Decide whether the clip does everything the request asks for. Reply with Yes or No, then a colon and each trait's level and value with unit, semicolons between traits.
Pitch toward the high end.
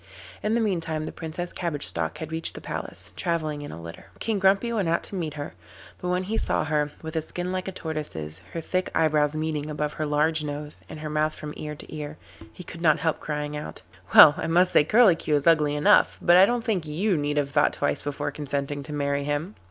No: medium, 155 Hz